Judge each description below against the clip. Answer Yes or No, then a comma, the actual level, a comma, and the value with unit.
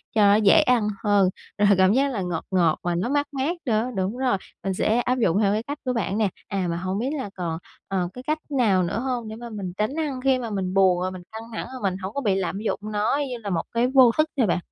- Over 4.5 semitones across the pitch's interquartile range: Yes, average, 4.9 semitones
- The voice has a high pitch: Yes, high, 210 Hz